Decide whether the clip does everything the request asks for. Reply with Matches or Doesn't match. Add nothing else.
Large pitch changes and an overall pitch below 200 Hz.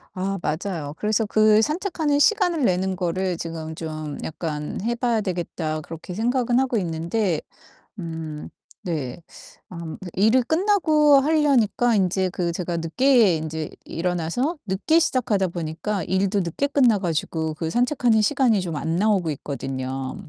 Matches